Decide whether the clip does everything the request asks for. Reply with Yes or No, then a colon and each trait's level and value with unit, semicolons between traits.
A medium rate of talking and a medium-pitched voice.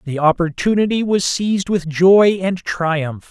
Yes: average, 145 wpm; medium, 180 Hz